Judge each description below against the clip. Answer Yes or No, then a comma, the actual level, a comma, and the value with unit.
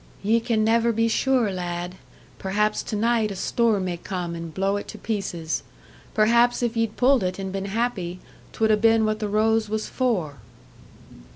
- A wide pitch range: No, average, 3.2 semitones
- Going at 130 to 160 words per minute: No, average, 180 wpm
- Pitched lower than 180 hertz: No, high, 215 Hz